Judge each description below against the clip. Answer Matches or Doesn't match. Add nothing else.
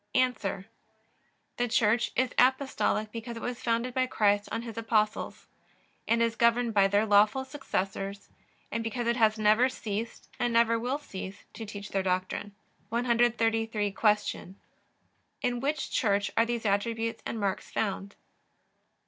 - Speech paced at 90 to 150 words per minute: Matches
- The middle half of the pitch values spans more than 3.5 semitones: Doesn't match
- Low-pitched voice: Doesn't match